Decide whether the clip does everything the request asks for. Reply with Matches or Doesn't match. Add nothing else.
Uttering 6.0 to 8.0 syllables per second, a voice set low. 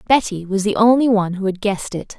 Doesn't match